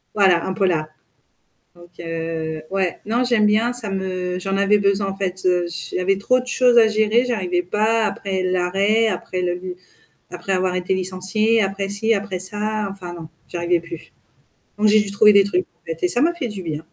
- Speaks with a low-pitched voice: No, high, 195 Hz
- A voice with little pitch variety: No, average, 3.0 semitones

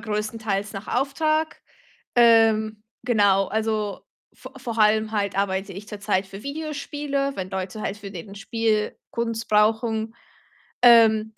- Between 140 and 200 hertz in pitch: No, high, 220 Hz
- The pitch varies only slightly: Yes, narrow, 2.3 semitones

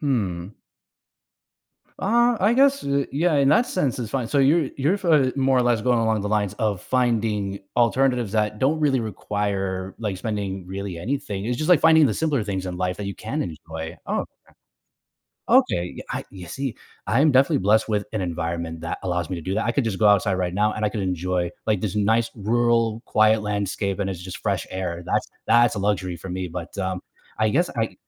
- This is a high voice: No, low, 105 Hz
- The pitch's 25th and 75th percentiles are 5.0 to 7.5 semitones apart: Yes, wide, 5.5 semitones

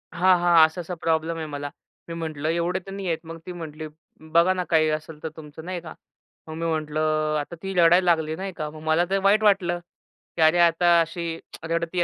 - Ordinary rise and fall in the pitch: No, narrow, 2.0 semitones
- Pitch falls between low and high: Yes, medium, 165 Hz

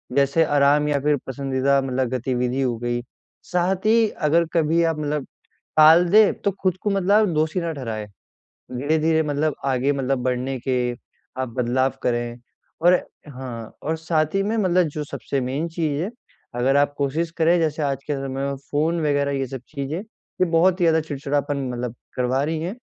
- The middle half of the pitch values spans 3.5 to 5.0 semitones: Yes, average, 3.8 semitones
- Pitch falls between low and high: Yes, medium, 145 Hz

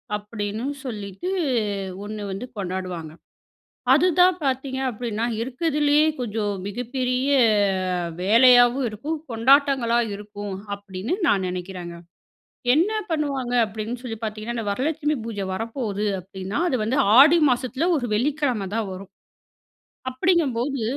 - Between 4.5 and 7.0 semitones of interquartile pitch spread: Yes, average, 5.0 semitones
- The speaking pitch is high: Yes, high, 235 Hz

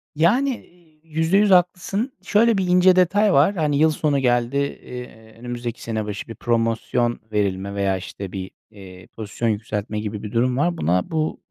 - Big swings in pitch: Yes, wide, 8.2 semitones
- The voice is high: No, low, 125 Hz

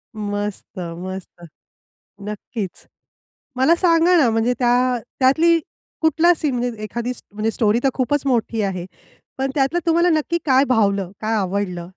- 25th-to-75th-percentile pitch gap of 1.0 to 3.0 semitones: No, wide, 5.5 semitones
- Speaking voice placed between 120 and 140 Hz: No, high, 240 Hz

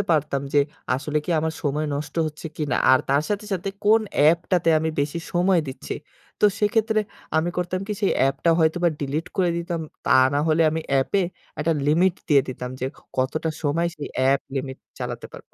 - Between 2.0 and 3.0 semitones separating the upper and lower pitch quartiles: No, average, 3.6 semitones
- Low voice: No, medium, 155 Hz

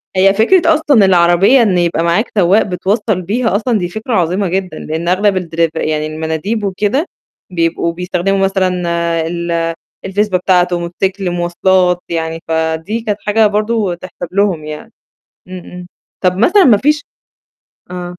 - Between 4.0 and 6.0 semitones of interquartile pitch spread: No, average, 3.3 semitones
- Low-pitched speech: No, medium, 185 Hz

